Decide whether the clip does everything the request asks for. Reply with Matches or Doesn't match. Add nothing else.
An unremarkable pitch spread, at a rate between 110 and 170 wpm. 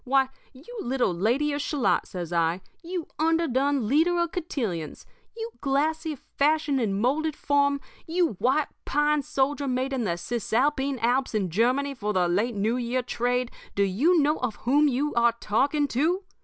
Matches